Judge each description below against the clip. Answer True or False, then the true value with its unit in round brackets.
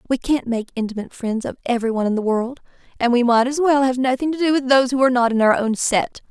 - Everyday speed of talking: False (275 wpm)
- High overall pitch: True (245 Hz)